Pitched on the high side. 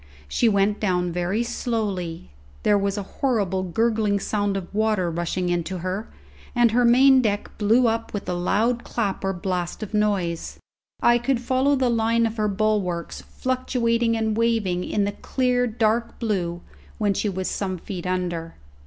Yes: high, 210 Hz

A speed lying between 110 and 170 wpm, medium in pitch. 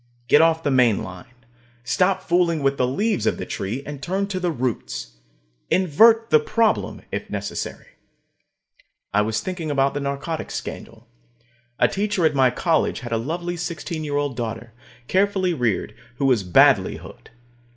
Yes: average, 160 wpm; medium, 145 Hz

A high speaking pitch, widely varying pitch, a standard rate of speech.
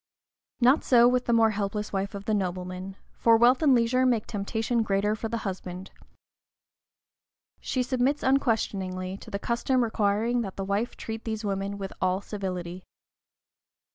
No: high, 215 Hz; average, 3.4 semitones; average, 155 wpm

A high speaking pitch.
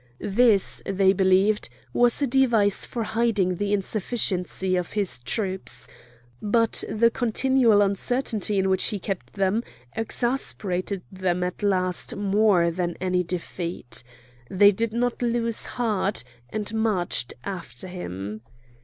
Yes: high, 200 Hz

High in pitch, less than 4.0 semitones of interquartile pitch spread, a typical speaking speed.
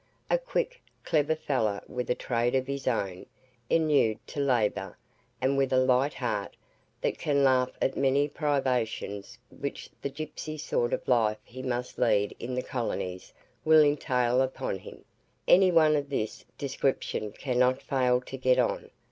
No: low, 130 Hz; average, 2.9 semitones; average, 160 wpm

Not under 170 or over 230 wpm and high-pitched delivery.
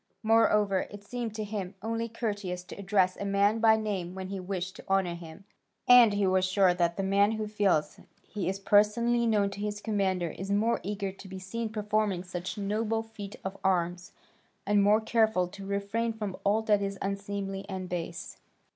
Yes: average, 190 wpm; high, 200 Hz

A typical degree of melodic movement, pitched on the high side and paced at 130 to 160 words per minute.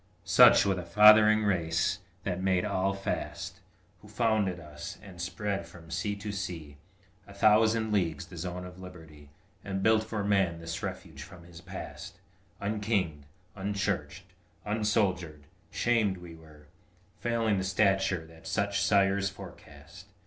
No: average, 3.3 semitones; very low, 95 Hz; average, 140 wpm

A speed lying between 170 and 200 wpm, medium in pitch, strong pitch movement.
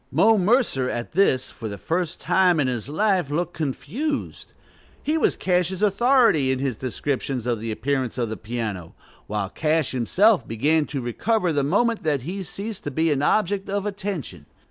Yes: average, 175 wpm; medium, 155 Hz; wide, 7.7 semitones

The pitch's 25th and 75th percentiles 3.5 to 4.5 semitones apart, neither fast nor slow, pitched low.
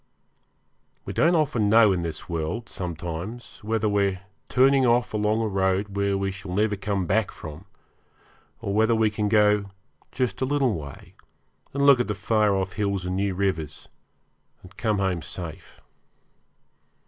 No: average, 3.0 semitones; average, 160 wpm; low, 100 Hz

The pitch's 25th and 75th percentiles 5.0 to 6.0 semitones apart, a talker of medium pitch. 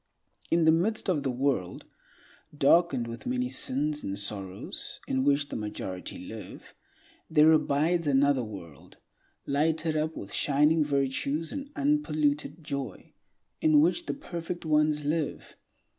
No: average, 3.6 semitones; medium, 150 Hz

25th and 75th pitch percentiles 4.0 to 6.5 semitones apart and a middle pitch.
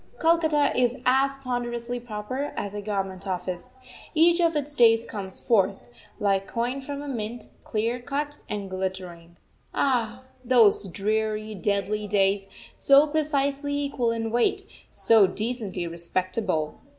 No: wide, 5.5 semitones; high, 225 Hz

